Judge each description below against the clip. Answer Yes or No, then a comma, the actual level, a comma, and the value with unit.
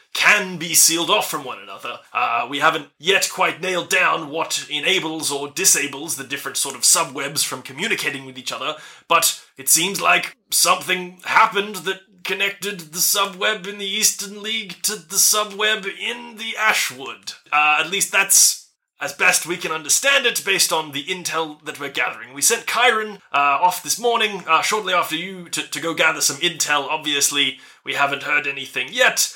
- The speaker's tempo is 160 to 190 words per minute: Yes, average, 180 wpm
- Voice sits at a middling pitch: Yes, medium, 180 Hz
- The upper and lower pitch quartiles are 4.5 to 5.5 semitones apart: Yes, average, 5.1 semitones